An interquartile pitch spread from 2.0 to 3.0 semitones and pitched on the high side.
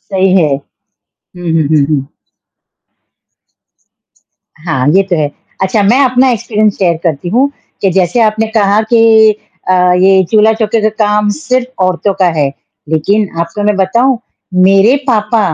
No: average, 3.7 semitones; high, 200 Hz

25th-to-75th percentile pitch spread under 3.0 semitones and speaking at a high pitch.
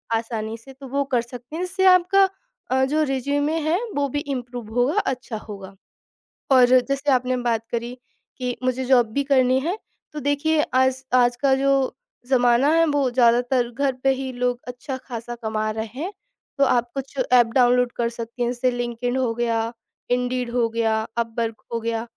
Yes: narrow, 2.4 semitones; very high, 250 Hz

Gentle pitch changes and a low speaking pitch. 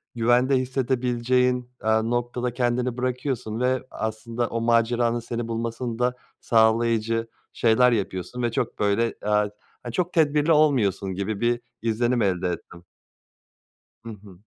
Yes: narrow, 2.0 semitones; low, 120 Hz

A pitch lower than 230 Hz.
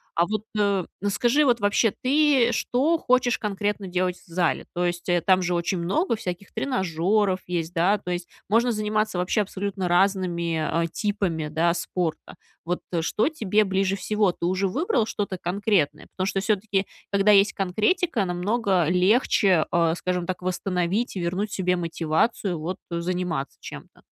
Yes: high, 190 Hz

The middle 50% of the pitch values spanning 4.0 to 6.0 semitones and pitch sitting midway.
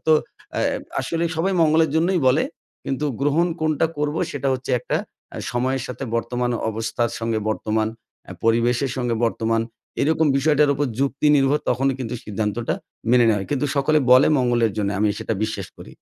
No: average, 4.3 semitones; low, 130 Hz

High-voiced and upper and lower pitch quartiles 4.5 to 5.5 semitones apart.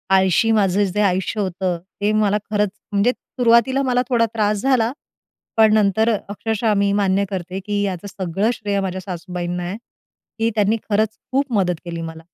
No: high, 205 Hz; average, 2.8 semitones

